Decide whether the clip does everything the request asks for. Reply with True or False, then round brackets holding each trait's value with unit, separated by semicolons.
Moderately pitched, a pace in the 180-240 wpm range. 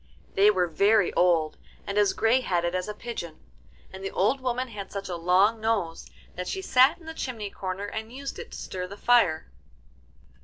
False (205 Hz; 195 wpm)